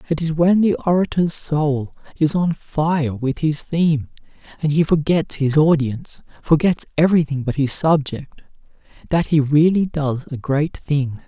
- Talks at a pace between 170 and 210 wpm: No, average, 155 wpm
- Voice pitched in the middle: Yes, medium, 150 Hz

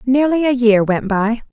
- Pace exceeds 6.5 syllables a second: No, 4.6 syllables/s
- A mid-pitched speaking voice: No, high, 240 Hz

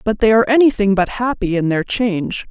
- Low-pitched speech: No, high, 215 Hz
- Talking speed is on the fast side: Yes, fast, 215 wpm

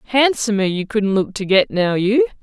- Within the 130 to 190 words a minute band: No, average, 200 wpm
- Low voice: No, high, 215 Hz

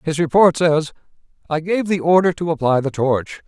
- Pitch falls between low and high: Yes, medium, 160 Hz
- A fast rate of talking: No, average, 190 wpm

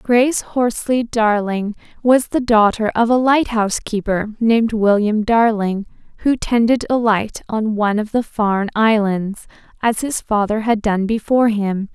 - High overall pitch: Yes, high, 220 Hz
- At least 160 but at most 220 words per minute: No, average, 150 wpm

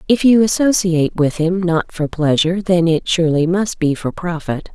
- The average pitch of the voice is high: No, medium, 175 Hz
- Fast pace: No, average, 190 wpm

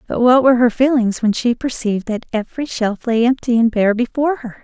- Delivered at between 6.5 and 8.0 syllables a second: No, 6.0 syllables/s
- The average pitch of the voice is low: No, high, 235 Hz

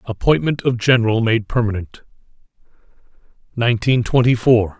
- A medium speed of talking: No, slow, 100 wpm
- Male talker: Yes, male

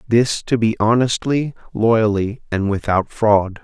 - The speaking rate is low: Yes, slow, 130 wpm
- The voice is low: Yes, low, 110 Hz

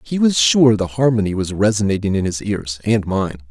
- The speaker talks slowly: No, fast, 205 wpm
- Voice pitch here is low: Yes, low, 105 Hz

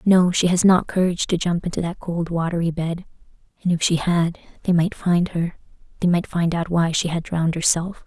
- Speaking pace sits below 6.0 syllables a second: Yes, 5.4 syllables/s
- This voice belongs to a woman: Yes, female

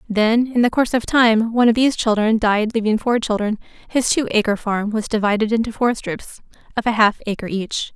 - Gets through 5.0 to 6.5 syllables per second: Yes, 5.5 syllables/s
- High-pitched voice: Yes, high, 225 Hz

